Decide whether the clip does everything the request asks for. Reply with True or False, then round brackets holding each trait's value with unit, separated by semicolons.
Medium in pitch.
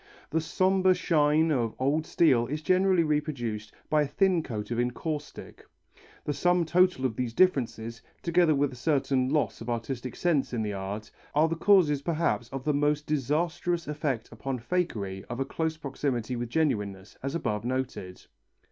True (145 Hz)